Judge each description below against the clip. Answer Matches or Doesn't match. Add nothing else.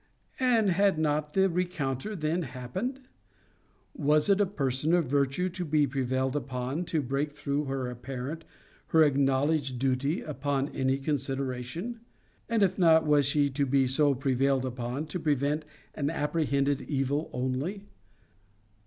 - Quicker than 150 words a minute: Doesn't match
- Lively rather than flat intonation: Doesn't match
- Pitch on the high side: Doesn't match